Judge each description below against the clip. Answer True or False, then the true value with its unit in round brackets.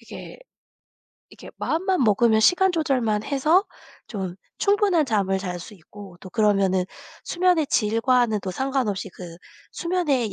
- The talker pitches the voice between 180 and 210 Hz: False (230 Hz)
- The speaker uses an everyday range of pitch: False (8.2 semitones)